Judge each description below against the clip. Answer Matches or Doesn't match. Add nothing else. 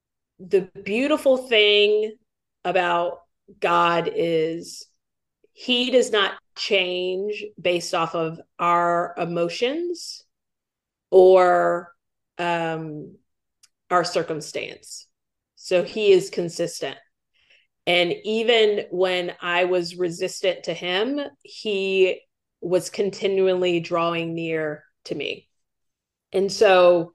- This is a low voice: Doesn't match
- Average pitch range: Matches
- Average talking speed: Doesn't match